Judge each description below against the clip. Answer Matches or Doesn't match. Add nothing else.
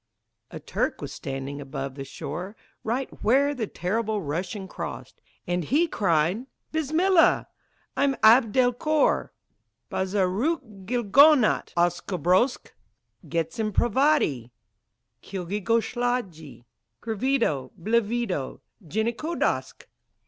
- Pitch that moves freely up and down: Matches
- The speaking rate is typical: Doesn't match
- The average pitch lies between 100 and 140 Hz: Doesn't match